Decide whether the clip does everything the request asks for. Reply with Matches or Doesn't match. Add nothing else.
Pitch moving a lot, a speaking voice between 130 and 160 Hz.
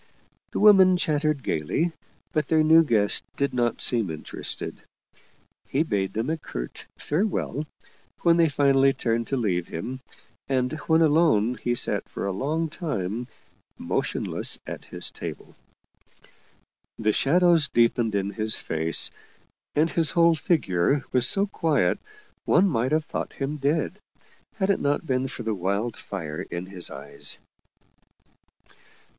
Matches